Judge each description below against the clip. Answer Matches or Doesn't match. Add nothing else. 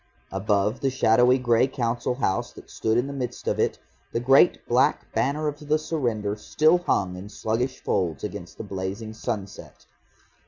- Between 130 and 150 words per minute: Doesn't match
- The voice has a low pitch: Matches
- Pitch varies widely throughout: Doesn't match